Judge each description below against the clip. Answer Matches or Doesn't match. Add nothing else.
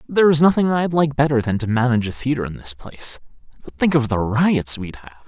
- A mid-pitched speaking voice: Doesn't match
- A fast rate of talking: Matches